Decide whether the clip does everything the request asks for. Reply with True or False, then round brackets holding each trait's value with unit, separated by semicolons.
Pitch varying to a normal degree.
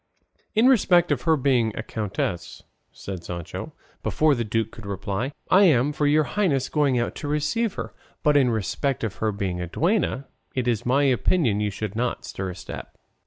False (6.2 semitones)